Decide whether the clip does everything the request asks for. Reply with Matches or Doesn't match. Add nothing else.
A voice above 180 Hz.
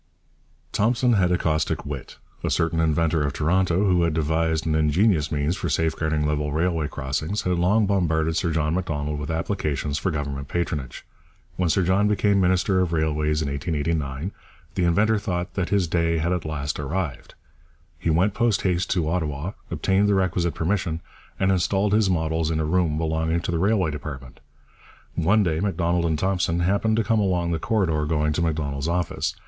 Doesn't match